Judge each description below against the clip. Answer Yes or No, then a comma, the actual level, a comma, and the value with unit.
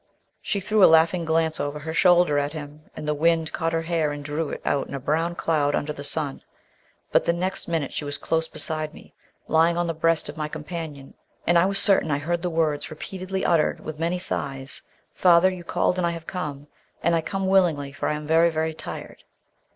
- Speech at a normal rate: No, fast, 220 wpm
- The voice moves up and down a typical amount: No, narrow, 2.3 semitones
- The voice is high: No, medium, 160 Hz